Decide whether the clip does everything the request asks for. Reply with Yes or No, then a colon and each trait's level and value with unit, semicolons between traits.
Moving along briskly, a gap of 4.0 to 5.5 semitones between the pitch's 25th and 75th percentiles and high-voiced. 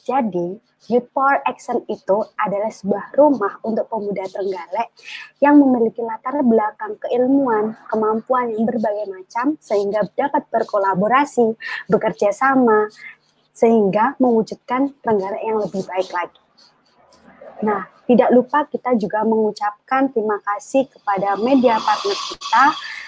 No: average, 115 wpm; average, 4.3 semitones; high, 225 Hz